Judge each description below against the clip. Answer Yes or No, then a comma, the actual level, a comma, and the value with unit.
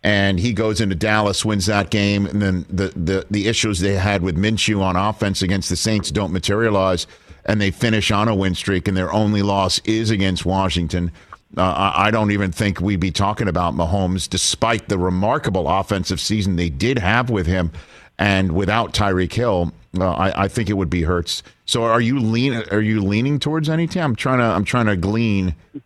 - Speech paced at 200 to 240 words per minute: Yes, fast, 205 wpm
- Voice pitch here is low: Yes, low, 100 Hz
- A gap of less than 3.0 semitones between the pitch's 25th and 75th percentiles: Yes, narrow, 2.6 semitones